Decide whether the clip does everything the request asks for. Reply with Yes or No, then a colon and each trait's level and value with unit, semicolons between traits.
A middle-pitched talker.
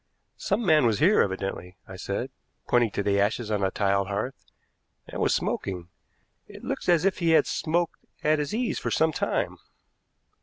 No: low, 120 Hz